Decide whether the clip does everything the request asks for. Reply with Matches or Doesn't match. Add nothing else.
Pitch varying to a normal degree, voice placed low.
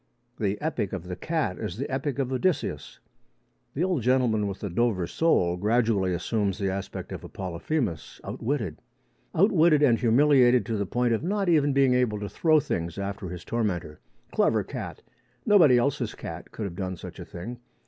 Doesn't match